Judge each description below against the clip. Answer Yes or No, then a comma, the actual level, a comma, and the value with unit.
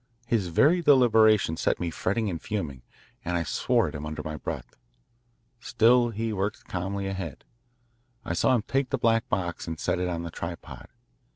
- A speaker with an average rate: Yes, average, 180 wpm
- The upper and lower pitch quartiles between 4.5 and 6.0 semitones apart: Yes, average, 5.2 semitones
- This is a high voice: No, very low, 95 Hz